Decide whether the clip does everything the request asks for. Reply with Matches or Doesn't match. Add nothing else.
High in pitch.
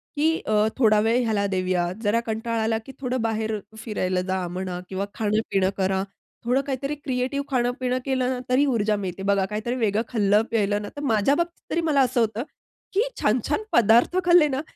Matches